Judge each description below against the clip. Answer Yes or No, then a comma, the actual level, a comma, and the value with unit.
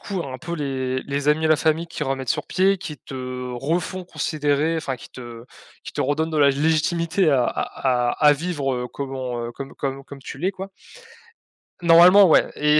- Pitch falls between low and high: Yes, medium, 145 Hz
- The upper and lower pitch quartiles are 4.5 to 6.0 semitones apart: No, average, 3.8 semitones